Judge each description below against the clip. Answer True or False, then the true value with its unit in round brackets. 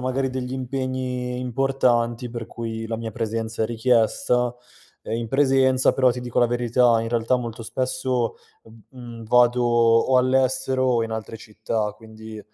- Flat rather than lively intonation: True (2.0 semitones)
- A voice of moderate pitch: False (120 Hz)